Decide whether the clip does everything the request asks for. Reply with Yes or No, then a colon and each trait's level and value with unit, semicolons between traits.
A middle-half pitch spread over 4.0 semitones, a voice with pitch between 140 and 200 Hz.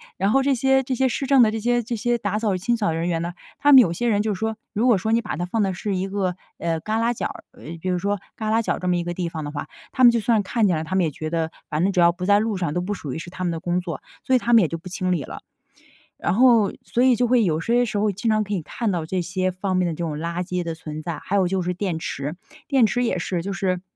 Yes: average, 4.6 semitones; high, 190 Hz